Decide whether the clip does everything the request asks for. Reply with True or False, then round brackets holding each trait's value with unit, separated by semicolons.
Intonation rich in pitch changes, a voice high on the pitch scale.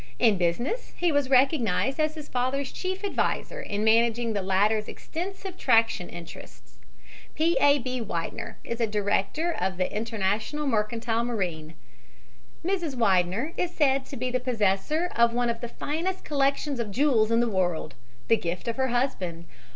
True (5.7 semitones; 235 Hz)